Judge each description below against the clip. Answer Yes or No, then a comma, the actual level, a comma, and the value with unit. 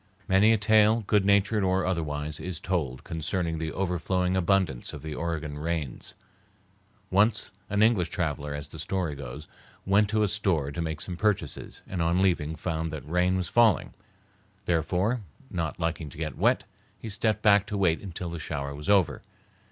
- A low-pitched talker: Yes, very low, 90 Hz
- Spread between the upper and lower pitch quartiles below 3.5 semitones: No, average, 4.1 semitones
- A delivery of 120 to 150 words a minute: No, average, 175 wpm